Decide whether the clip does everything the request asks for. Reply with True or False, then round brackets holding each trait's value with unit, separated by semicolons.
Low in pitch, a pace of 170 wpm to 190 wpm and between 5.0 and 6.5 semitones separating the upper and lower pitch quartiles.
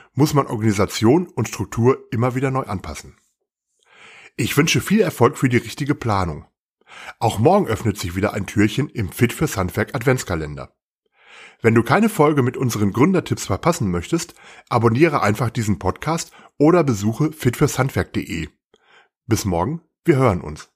False (120 Hz; 135 wpm; 5.6 semitones)